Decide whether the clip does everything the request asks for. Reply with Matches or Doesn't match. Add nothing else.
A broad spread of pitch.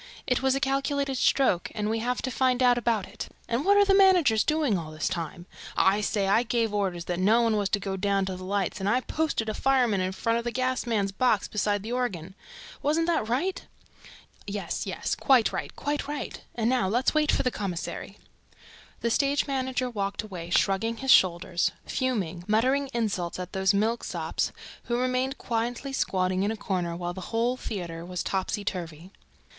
Doesn't match